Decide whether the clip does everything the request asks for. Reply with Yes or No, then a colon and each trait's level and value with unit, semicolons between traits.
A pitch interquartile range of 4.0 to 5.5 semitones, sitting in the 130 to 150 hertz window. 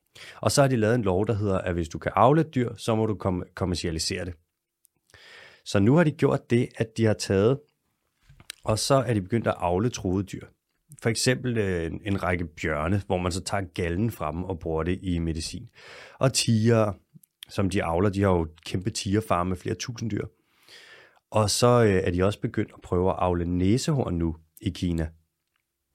No: average, 4.4 semitones; low, 100 Hz